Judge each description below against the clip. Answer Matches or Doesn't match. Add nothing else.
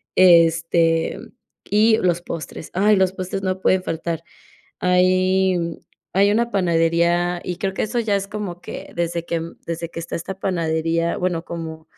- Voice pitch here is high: Doesn't match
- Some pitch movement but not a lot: Doesn't match